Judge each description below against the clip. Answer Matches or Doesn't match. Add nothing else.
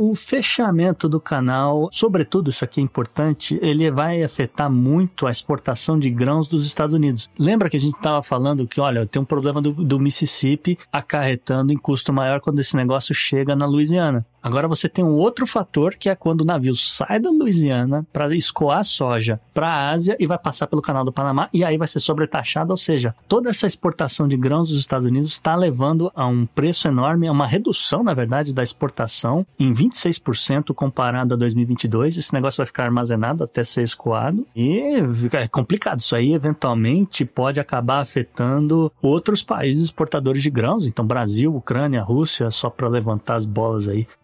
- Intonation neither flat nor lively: Matches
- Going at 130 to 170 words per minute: Doesn't match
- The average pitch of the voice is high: Doesn't match